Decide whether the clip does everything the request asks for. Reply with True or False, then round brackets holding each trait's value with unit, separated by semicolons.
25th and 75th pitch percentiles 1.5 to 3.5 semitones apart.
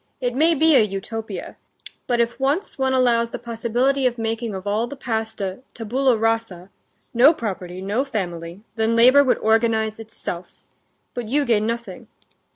True (2.8 semitones)